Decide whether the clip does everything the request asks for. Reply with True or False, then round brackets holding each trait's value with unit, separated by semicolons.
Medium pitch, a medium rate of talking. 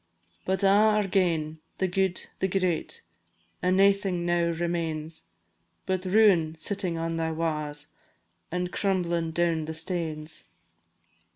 False (175 Hz; 120 wpm)